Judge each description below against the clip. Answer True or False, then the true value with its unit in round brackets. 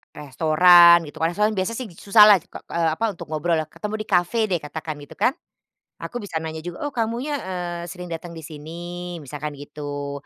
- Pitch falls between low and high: True (170 Hz)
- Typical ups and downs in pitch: True (3.6 semitones)